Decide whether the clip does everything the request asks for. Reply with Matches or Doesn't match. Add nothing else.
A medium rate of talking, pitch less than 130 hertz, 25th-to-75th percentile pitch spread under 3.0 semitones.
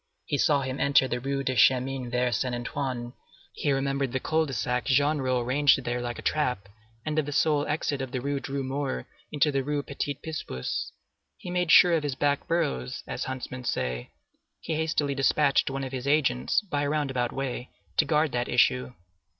Doesn't match